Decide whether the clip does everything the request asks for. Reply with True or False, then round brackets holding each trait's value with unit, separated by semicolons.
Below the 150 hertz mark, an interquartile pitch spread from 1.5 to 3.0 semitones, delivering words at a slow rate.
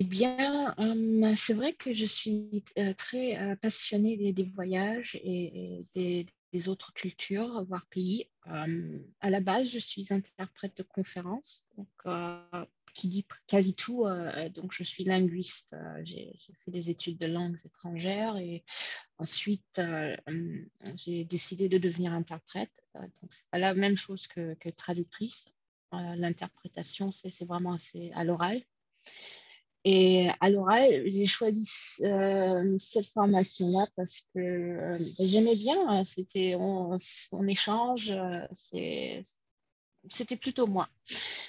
False (190 Hz; 2.7 semitones; 140 wpm)